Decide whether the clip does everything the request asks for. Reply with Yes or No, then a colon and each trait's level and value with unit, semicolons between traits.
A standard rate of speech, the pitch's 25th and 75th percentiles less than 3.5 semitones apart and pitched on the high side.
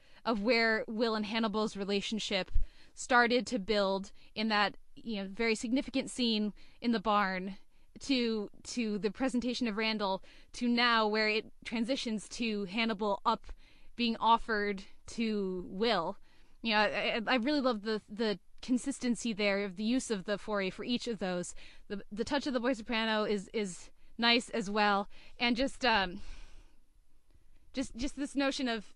Yes: average, 160 wpm; average, 2.7 semitones; high, 225 Hz